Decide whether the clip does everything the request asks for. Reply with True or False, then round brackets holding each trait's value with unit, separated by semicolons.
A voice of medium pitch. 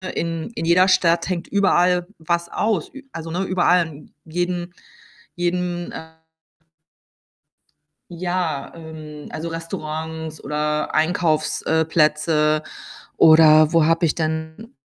True (165 Hz)